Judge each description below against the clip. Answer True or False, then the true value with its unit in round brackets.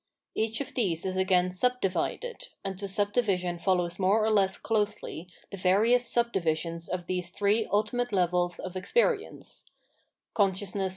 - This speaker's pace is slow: False (150 wpm)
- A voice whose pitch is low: False (195 Hz)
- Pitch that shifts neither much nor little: True (3.3 semitones)